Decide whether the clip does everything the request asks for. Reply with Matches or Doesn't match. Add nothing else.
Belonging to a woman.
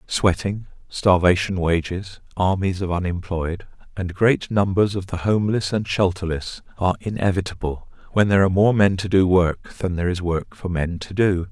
Doesn't match